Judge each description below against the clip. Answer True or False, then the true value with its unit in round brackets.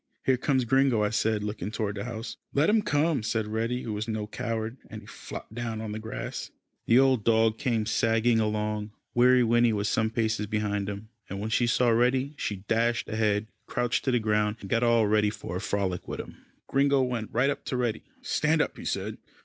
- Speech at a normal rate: False (215 wpm)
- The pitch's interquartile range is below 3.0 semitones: True (2.5 semitones)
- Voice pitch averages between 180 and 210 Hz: False (110 Hz)